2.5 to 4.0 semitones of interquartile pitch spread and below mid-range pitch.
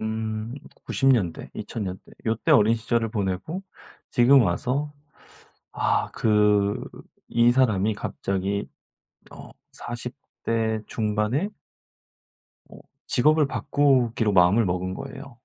Yes: average, 3.4 semitones; low, 110 Hz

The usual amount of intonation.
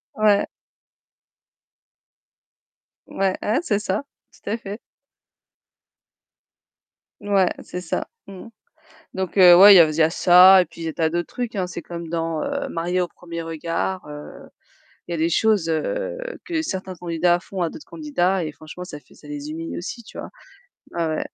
Yes: average, 3.2 semitones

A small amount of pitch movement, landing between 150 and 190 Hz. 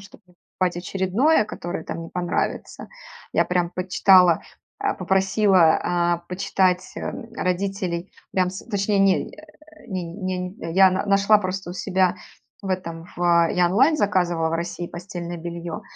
Yes: narrow, 2.1 semitones; medium, 185 Hz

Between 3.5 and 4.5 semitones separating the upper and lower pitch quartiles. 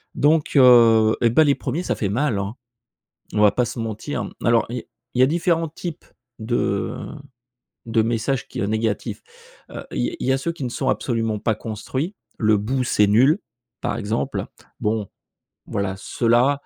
Yes: average, 3.9 semitones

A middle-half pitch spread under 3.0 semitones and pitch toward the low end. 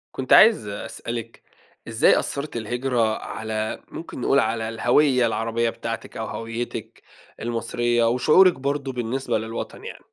Yes: narrow, 2.6 semitones; low, 115 Hz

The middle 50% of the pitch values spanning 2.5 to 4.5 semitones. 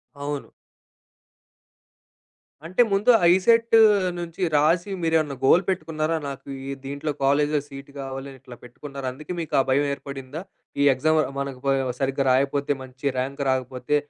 Yes: average, 2.9 semitones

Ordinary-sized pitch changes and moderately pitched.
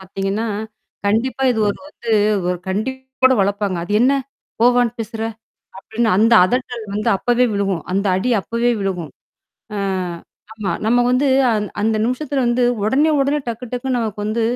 No: average, 3.7 semitones; high, 230 Hz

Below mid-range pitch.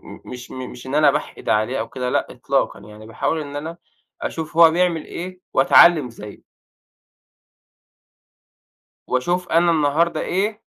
No: medium, 155 Hz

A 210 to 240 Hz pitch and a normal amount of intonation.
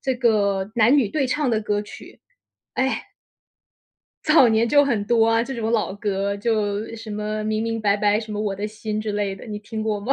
No: high, 215 Hz; narrow, 2.0 semitones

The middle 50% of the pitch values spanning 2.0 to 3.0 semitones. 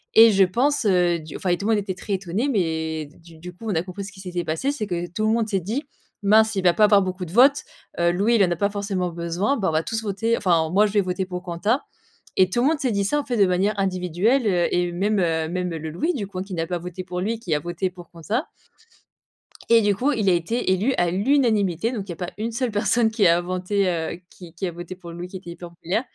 No: average, 3.7 semitones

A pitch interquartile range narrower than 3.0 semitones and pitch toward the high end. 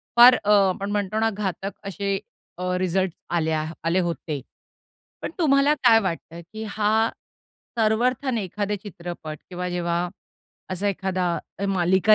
No: average, 3.7 semitones; high, 195 Hz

